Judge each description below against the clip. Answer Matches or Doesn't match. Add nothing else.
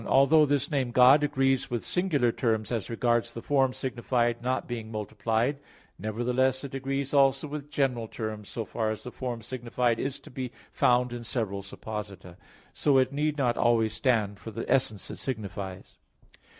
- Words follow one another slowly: Doesn't match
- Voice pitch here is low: Matches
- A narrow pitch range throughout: Doesn't match